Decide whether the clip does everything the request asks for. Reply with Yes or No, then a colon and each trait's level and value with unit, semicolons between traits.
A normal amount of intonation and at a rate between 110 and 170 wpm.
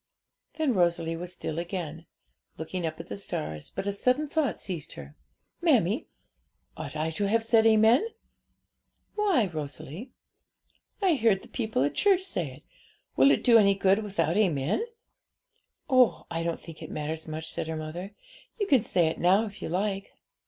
No: wide, 5.8 semitones; average, 165 wpm